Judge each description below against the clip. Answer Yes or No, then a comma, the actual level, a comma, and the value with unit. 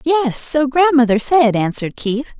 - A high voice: Yes, very high, 265 Hz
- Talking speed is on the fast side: No, average, 150 wpm